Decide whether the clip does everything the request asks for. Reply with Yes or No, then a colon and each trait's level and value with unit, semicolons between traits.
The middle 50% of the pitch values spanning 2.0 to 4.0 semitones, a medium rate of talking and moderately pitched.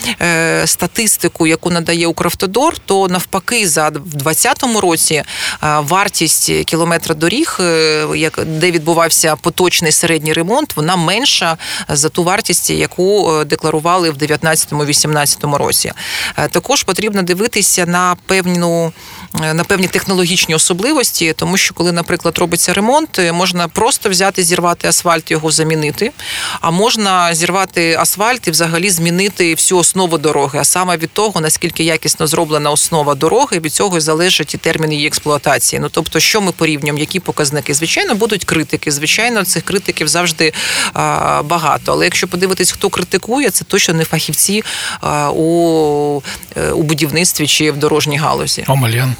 Yes: average, 2.9 semitones; average, 135 wpm; medium, 170 Hz